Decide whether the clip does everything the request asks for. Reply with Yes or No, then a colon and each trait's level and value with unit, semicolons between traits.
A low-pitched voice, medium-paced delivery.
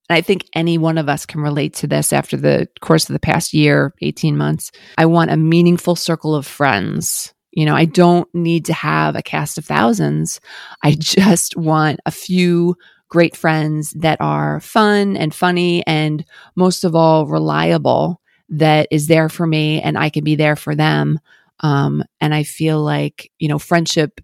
No: medium, 155 Hz; average, 185 wpm